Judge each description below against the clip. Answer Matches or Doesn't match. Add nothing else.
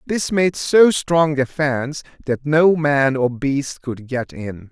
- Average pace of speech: Matches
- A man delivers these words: Matches